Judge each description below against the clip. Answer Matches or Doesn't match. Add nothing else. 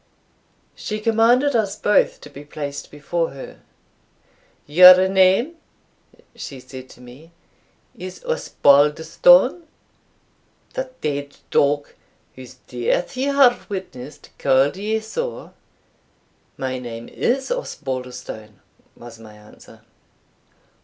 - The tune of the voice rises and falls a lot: Matches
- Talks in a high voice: Doesn't match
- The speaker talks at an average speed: Doesn't match